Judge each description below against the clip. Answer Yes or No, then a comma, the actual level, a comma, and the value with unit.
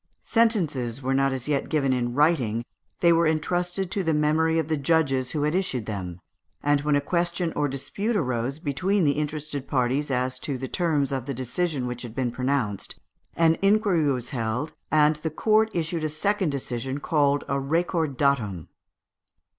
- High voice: No, medium, 145 Hz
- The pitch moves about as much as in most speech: Yes, average, 4.0 semitones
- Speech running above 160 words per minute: Yes, average, 175 wpm